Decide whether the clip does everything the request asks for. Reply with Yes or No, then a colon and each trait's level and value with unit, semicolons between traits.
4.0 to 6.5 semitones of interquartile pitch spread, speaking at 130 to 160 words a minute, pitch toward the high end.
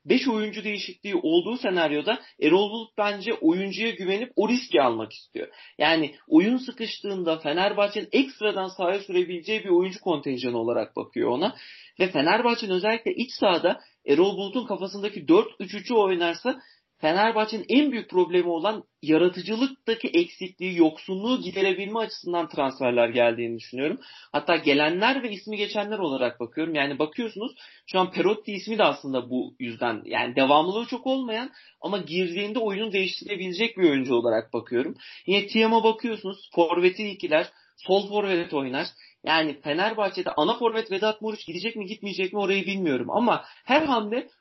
Yes: average, 4.8 semitones; fast, 140 wpm; high, 200 Hz